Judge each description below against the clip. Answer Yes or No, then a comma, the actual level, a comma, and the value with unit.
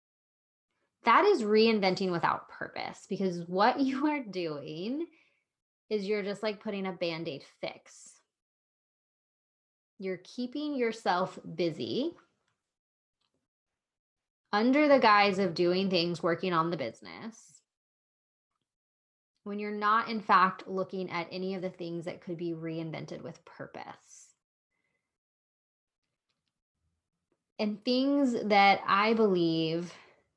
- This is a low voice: No, medium, 185 Hz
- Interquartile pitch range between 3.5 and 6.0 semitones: Yes, average, 4.4 semitones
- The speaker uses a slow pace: Yes, slow, 110 wpm